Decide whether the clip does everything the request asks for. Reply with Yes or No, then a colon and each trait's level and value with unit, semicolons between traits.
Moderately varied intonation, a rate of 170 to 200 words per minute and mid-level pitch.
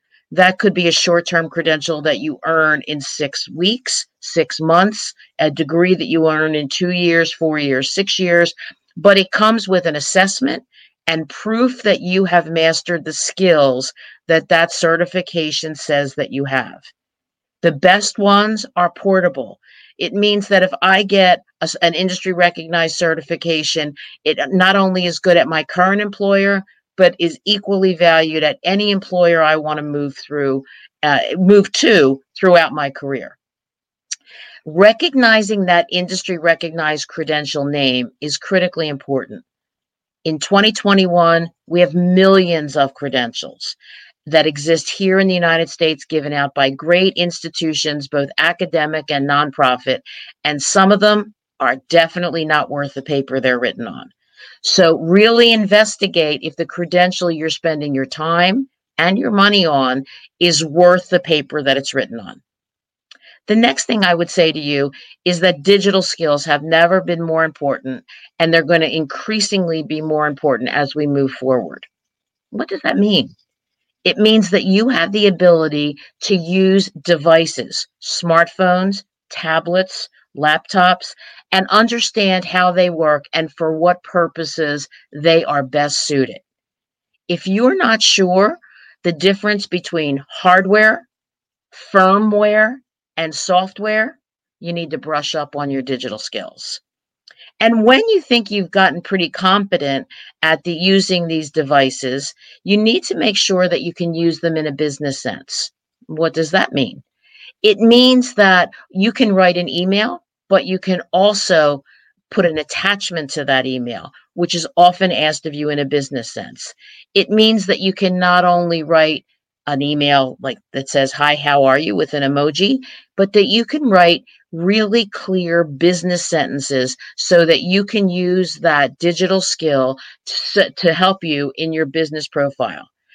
No: average, 4.0 semitones; average, 155 wpm; medium, 170 Hz